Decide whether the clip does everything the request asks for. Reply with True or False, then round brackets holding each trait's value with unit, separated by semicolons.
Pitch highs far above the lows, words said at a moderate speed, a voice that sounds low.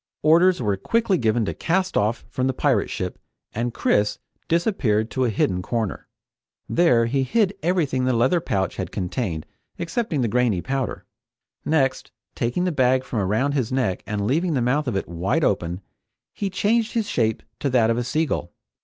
True (7.1 semitones; 180 wpm; 125 Hz)